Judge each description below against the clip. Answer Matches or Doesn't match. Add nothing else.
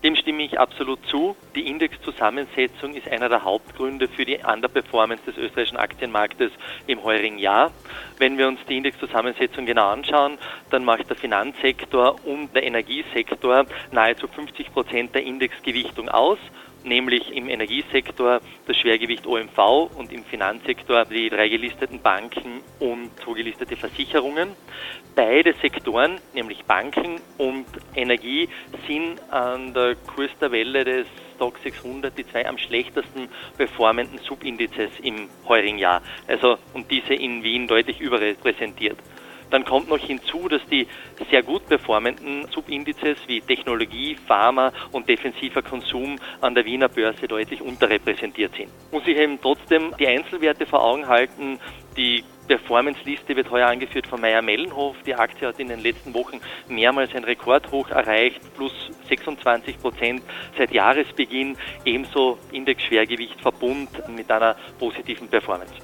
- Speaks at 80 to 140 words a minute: Matches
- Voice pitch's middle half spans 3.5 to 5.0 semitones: Doesn't match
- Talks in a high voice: Doesn't match